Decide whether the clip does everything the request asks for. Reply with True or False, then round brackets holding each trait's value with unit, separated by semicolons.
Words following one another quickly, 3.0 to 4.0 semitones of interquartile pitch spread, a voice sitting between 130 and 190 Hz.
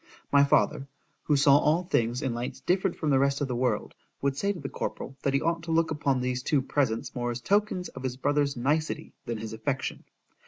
True (225 wpm; 3.4 semitones; 140 Hz)